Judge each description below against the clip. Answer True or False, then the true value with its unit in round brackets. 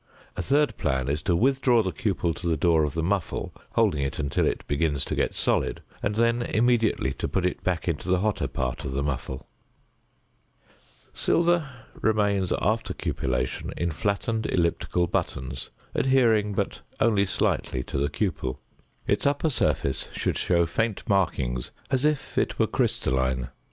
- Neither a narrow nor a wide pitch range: False (7.9 semitones)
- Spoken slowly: False (160 wpm)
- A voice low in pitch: True (90 Hz)